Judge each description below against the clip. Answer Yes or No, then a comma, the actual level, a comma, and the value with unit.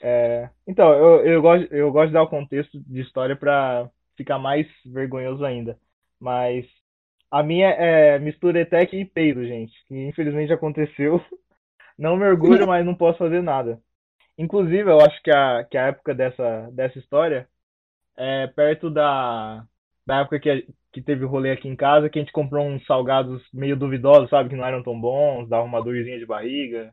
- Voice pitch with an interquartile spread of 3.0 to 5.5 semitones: Yes, average, 3.7 semitones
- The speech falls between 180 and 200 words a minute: Yes, fast, 185 wpm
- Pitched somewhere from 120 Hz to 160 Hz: Yes, medium, 140 Hz